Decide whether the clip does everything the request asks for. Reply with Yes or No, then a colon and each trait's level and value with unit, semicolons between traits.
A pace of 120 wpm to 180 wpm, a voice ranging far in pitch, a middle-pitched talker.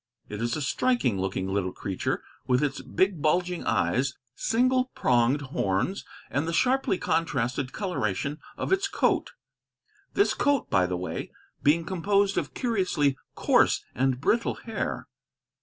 Yes: average, 140 wpm; wide, 8.5 semitones; medium, 150 Hz